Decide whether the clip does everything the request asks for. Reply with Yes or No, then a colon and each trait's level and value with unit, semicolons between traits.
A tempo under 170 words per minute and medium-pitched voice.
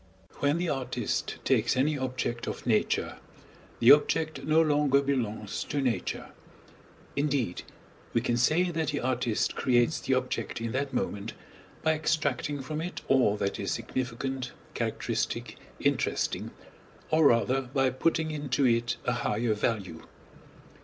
No: slow, 135 wpm; low, 130 Hz